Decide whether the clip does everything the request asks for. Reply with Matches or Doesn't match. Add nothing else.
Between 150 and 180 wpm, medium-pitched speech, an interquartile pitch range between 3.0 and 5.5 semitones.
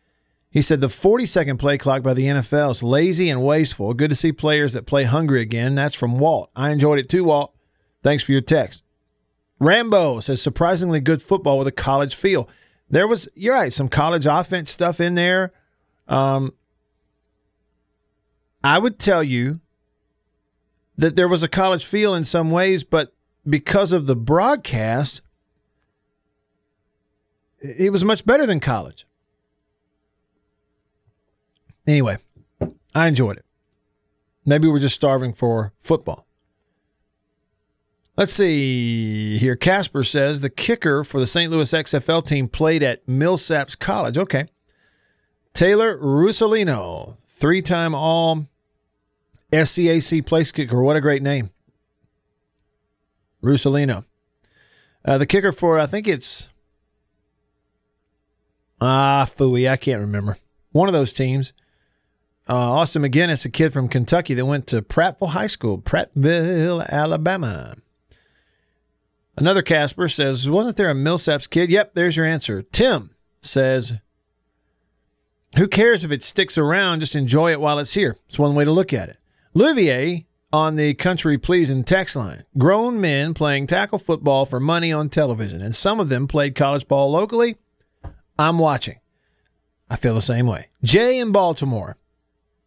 Doesn't match